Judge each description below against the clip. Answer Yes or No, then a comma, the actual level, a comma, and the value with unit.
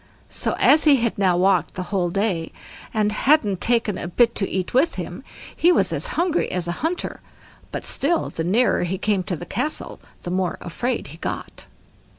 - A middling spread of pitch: No, wide, 6.2 semitones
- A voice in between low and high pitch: No, high, 200 Hz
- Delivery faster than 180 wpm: Yes, average, 190 wpm